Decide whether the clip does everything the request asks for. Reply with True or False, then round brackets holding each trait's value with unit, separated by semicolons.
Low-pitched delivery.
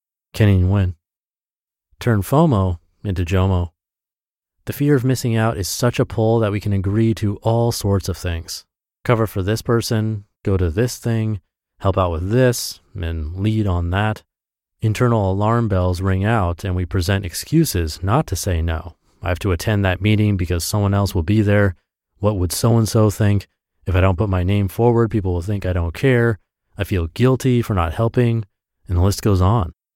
True (100 Hz)